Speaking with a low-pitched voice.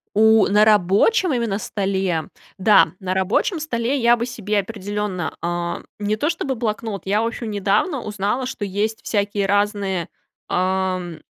No: high, 205 Hz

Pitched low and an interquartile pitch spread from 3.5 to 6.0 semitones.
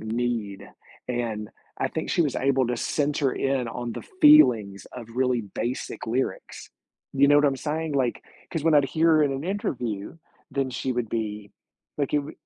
Yes: low, 130 Hz; average, 3.9 semitones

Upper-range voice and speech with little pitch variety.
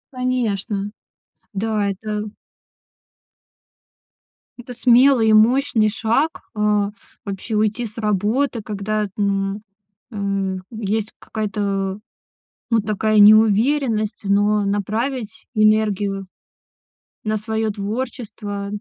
Yes: high, 215 Hz; narrow, 1.9 semitones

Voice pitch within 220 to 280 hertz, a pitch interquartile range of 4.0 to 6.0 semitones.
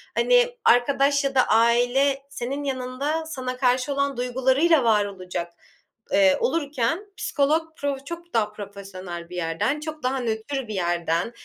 Yes: very high, 255 Hz; average, 5.2 semitones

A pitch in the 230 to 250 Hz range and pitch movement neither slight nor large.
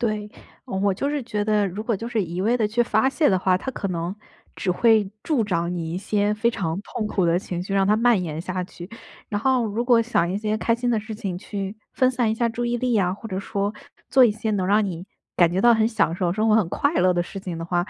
No: high, 210 Hz; average, 3.9 semitones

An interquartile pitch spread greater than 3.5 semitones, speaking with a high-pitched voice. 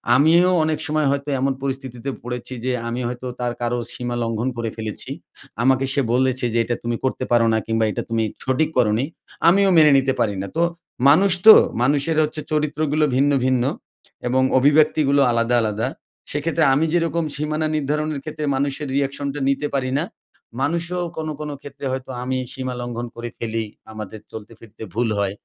No: average, 4.0 semitones; low, 135 Hz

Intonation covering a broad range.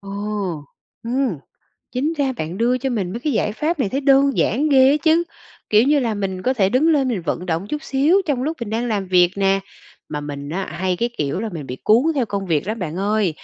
Yes: wide, 6.3 semitones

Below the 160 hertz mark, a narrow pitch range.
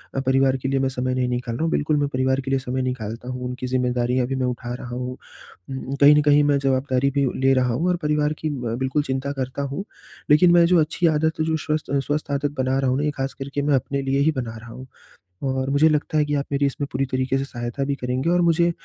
Yes: low, 135 Hz; narrow, 2.3 semitones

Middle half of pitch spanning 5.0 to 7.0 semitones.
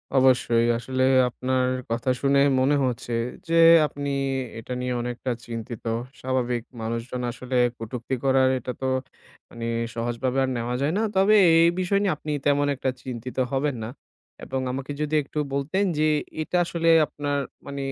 No: average, 2.7 semitones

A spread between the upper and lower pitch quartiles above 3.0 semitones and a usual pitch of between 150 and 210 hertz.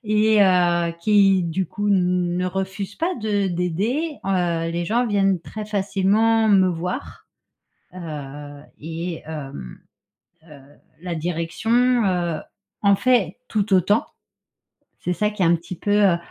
Yes: average, 3.4 semitones; medium, 185 Hz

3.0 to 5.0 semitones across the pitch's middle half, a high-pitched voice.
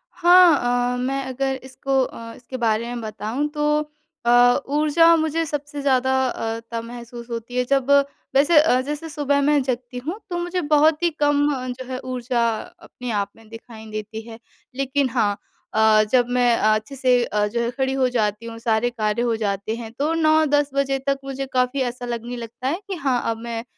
Yes: average, 3.5 semitones; very high, 250 Hz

